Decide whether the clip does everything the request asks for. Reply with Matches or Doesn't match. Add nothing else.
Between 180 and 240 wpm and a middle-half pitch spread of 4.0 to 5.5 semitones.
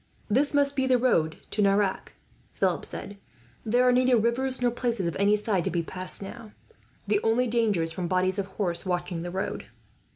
Matches